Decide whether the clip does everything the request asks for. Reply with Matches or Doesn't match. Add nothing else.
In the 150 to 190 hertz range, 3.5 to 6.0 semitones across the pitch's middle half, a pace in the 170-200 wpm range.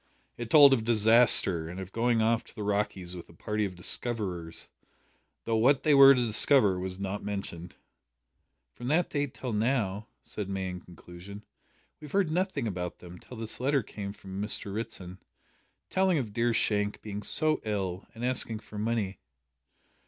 Doesn't match